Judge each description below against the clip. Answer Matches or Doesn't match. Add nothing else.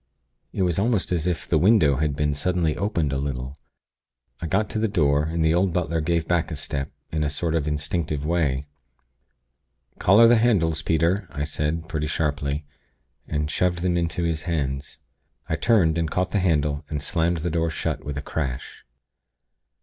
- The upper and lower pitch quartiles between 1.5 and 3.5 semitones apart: Matches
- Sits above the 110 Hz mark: Doesn't match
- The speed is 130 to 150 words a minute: Doesn't match